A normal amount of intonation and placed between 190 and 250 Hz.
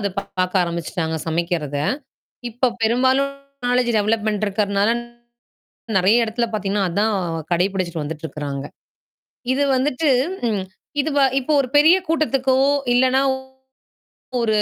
No: wide, 6.0 semitones; high, 215 Hz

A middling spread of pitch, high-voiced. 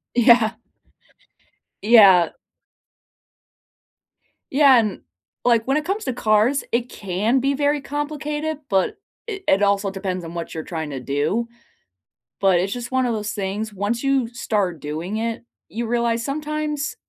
No: wide, 5.9 semitones; high, 230 Hz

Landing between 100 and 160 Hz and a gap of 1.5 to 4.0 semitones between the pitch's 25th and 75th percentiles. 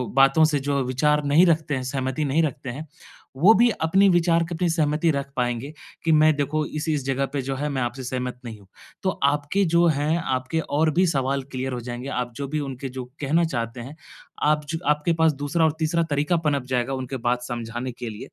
Yes: medium, 140 Hz; average, 3.4 semitones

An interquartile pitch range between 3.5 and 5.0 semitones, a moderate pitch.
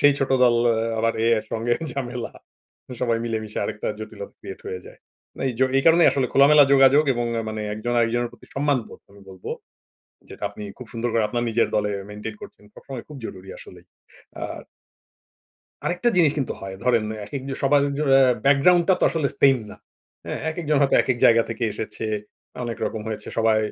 No: average, 4.0 semitones; low, 120 Hz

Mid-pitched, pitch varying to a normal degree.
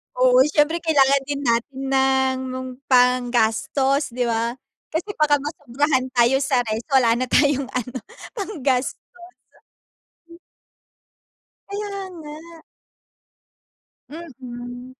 No: very high, 260 Hz; average, 3.0 semitones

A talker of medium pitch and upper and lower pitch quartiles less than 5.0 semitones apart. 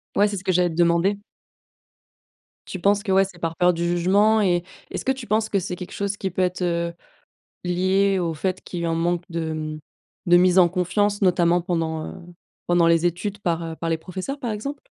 Yes: medium, 180 Hz; narrow, 2.6 semitones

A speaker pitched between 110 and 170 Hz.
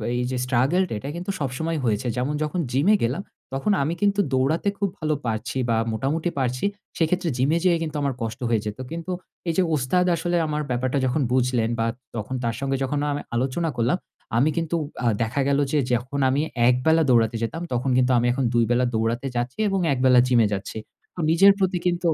Yes: low, 135 Hz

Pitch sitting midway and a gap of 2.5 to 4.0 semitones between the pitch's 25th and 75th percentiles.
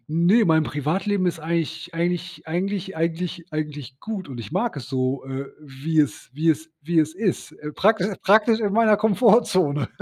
No: medium, 165 Hz; average, 4.6 semitones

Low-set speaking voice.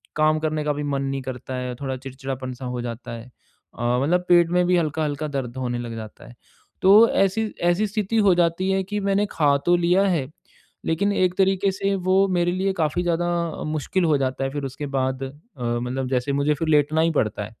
No: medium, 155 Hz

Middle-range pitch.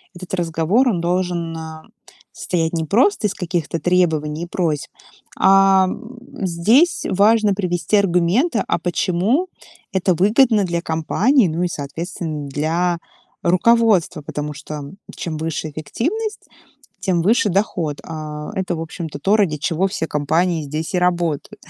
Yes: medium, 175 Hz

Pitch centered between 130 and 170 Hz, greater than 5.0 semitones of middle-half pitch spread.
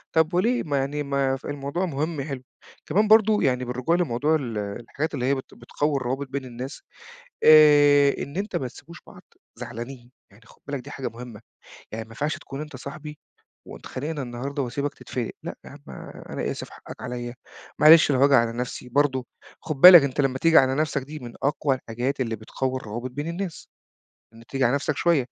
No: medium, 140 Hz; average, 3.4 semitones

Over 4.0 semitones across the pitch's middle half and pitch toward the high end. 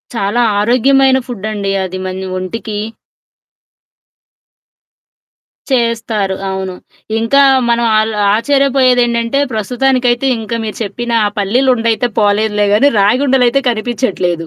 No: average, 3.5 semitones; high, 230 Hz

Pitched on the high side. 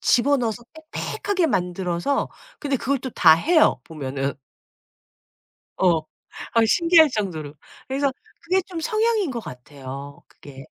Yes: high, 230 Hz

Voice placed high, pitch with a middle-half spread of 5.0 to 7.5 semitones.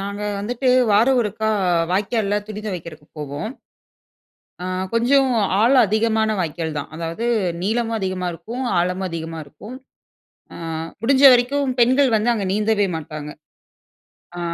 Yes: high, 210 Hz; average, 5.3 semitones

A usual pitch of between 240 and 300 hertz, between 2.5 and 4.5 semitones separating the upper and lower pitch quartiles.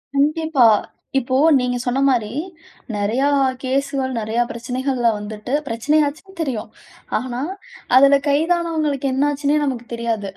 Yes: very high, 260 Hz; average, 3.4 semitones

